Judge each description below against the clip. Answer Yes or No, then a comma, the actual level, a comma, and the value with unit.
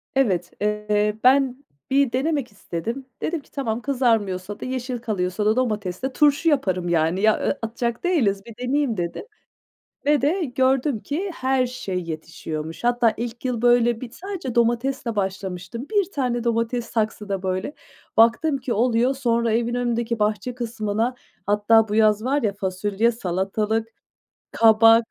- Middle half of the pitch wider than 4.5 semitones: No, average, 3.7 semitones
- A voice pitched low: No, high, 230 Hz